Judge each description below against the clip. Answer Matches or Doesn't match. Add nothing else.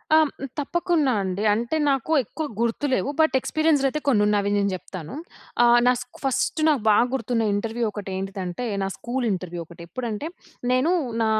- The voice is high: Matches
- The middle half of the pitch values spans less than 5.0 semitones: Doesn't match